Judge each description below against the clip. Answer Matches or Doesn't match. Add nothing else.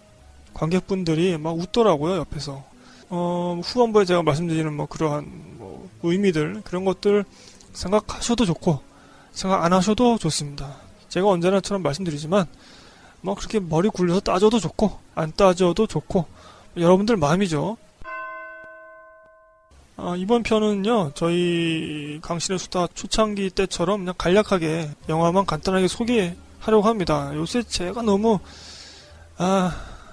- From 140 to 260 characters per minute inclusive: Doesn't match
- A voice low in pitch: Doesn't match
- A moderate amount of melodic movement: Matches